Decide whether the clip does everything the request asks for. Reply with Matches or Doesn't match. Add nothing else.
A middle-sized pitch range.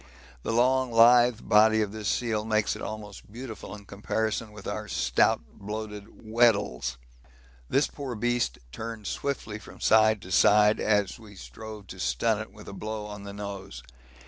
Doesn't match